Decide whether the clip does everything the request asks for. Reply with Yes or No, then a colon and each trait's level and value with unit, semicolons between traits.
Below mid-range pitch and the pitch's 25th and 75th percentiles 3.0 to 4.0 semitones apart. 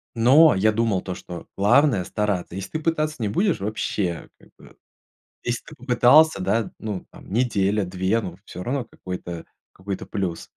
No: low, 105 Hz; average, 4.6 semitones